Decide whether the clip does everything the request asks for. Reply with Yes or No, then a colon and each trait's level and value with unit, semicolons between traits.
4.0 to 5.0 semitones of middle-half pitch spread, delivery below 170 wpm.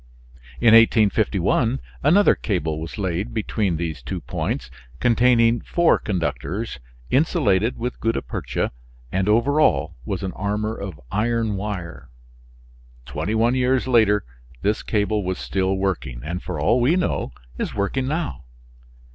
Yes: average, 4.3 semitones; slow, 135 wpm